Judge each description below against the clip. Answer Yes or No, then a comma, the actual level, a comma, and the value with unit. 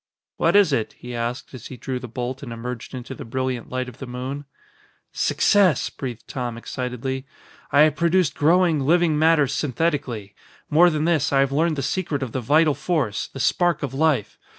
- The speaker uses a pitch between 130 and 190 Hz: Yes, low, 135 Hz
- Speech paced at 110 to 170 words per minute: No, average, 190 wpm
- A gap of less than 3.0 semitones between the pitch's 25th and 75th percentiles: No, average, 3.9 semitones